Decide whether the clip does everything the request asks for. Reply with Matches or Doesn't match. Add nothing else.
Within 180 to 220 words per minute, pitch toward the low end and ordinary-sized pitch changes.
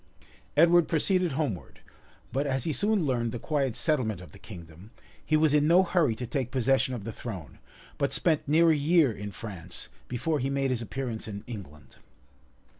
Doesn't match